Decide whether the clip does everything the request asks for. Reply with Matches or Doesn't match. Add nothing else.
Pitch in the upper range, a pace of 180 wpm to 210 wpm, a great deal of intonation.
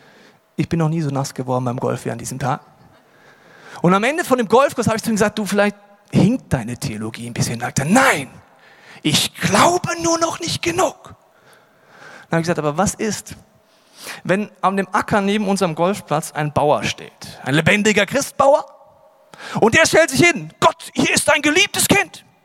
Matches